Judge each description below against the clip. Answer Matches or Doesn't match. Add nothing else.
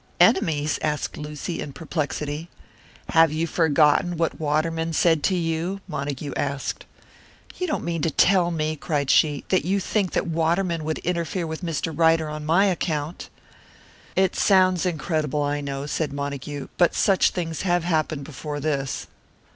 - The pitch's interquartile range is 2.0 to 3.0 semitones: Matches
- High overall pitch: Doesn't match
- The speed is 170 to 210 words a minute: Doesn't match